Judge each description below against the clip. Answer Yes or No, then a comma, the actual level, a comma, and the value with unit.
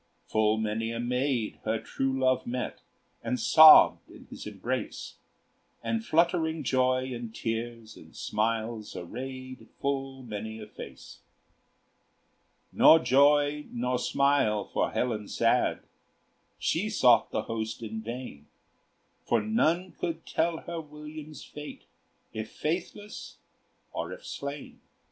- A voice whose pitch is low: Yes, low, 130 Hz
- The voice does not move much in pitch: No, average, 5.2 semitones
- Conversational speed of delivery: No, slow, 120 wpm